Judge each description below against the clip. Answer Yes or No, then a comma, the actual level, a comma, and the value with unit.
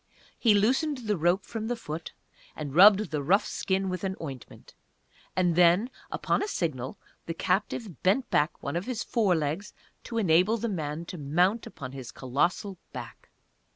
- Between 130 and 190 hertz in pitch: Yes, medium, 185 Hz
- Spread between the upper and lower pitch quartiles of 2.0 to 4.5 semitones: No, average, 5.1 semitones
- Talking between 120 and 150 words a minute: No, average, 170 wpm